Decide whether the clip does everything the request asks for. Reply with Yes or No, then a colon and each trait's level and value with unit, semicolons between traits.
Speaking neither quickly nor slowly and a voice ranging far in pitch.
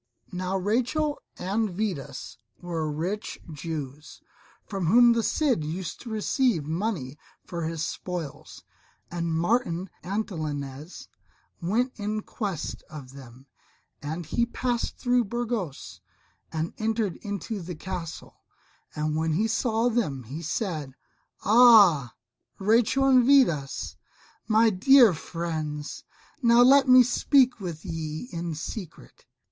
No: slow, 120 wpm; wide, 6.5 semitones